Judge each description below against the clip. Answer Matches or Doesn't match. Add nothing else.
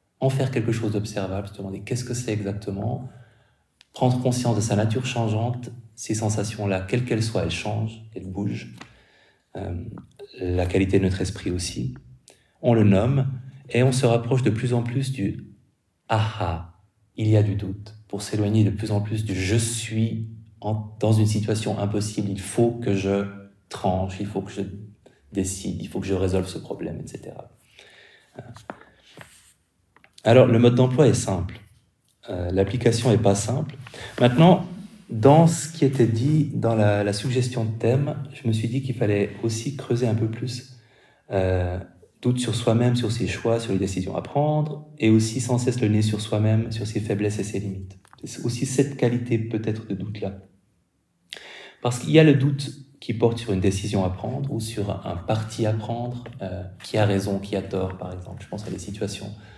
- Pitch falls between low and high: Doesn't match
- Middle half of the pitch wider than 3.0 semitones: Matches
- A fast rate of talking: Doesn't match